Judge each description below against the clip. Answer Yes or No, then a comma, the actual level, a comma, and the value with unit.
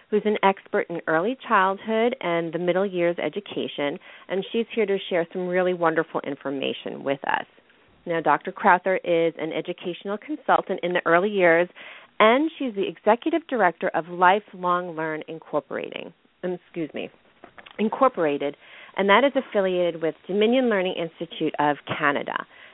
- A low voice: No, medium, 180 Hz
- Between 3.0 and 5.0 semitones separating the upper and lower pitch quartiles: Yes, average, 4.0 semitones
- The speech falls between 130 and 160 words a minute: Yes, average, 150 wpm